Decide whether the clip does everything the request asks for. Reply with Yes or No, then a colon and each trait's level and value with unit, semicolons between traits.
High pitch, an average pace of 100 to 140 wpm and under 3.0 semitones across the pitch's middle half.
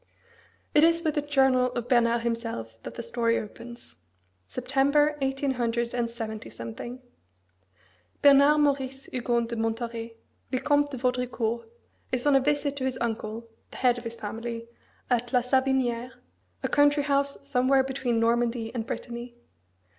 Yes: high, 245 Hz; slow, 135 wpm; narrow, 2.6 semitones